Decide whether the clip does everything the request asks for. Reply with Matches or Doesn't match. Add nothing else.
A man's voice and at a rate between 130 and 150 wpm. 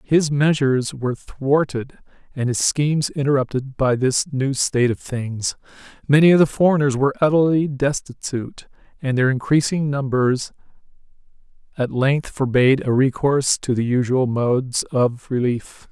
Matches